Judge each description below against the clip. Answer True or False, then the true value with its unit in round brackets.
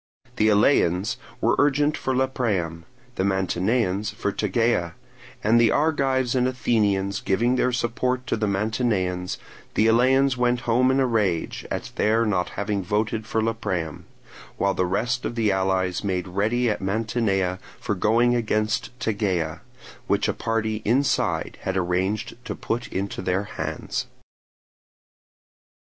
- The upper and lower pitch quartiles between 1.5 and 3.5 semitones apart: False (4.1 semitones)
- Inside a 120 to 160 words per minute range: True (140 wpm)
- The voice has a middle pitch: False (110 Hz)